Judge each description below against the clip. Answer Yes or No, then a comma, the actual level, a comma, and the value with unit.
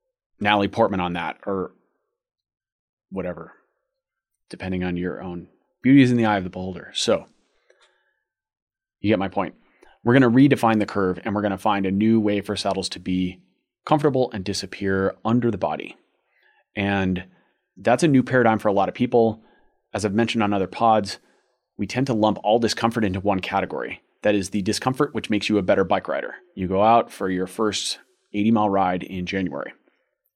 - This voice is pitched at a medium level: No, low, 105 Hz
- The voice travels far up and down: No, average, 3.4 semitones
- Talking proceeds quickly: No, average, 185 wpm